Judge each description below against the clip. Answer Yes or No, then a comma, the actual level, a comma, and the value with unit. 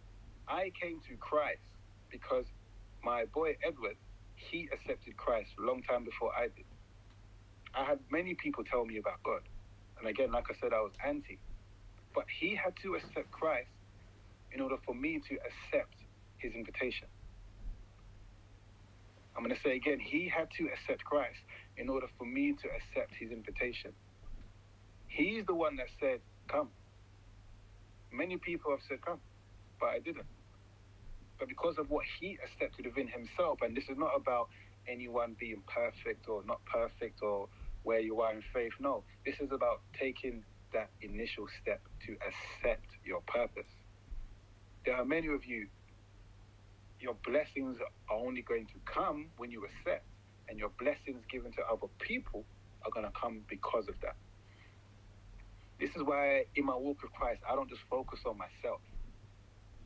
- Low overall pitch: Yes, low, 105 Hz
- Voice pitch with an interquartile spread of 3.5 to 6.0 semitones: Yes, average, 4.0 semitones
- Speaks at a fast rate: No, average, 160 wpm